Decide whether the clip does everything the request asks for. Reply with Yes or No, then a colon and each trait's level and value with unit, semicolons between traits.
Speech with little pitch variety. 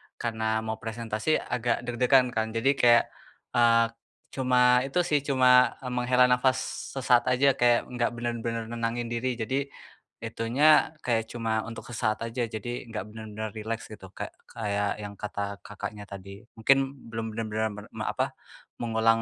Yes: narrow, 2.1 semitones